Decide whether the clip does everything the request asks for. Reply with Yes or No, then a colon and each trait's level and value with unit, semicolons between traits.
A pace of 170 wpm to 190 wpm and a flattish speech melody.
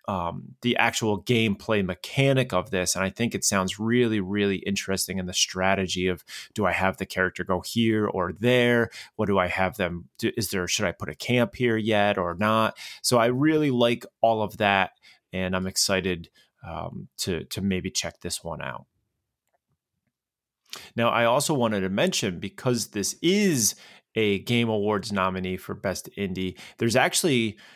No: average, 175 wpm; average, 3.8 semitones